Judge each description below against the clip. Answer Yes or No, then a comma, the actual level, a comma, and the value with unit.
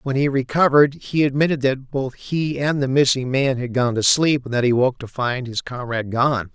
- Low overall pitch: Yes, low, 130 Hz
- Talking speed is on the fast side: Yes, fast, 230 wpm